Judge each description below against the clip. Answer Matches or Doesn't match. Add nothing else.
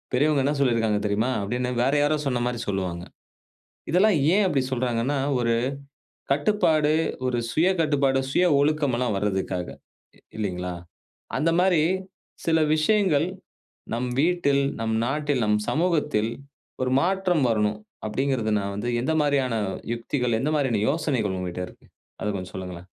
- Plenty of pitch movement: Matches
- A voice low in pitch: Matches